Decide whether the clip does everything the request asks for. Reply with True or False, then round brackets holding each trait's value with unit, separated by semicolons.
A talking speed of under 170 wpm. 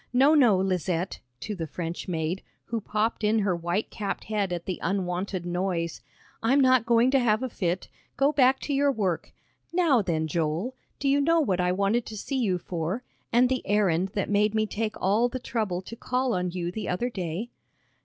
False (200 wpm)